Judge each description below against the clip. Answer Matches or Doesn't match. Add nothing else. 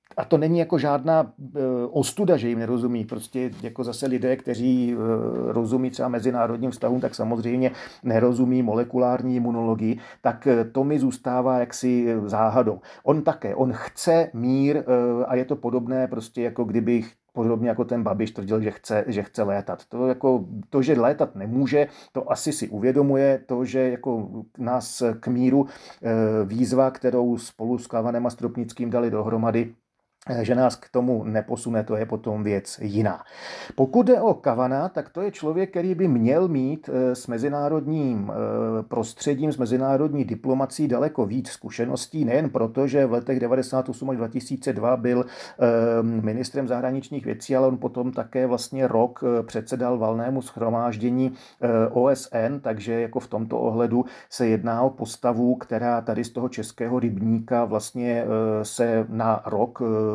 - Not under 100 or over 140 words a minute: Doesn't match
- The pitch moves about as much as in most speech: Doesn't match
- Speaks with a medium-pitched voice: Doesn't match